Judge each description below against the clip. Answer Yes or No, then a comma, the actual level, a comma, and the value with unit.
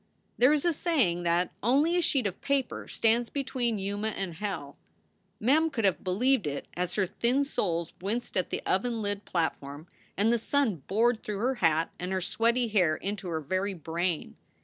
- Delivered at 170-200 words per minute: Yes, average, 185 wpm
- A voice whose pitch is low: No, high, 205 Hz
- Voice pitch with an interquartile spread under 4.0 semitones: No, wide, 5.6 semitones